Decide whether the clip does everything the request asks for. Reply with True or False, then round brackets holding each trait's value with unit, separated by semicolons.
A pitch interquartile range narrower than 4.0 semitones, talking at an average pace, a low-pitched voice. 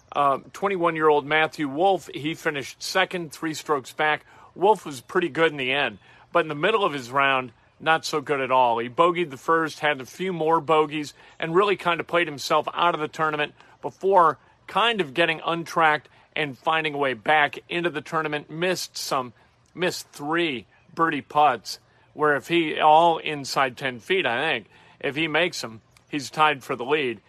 False (3.0 semitones; 190 wpm; 155 Hz)